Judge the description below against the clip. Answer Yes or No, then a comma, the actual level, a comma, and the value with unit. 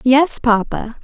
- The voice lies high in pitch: Yes, high, 240 Hz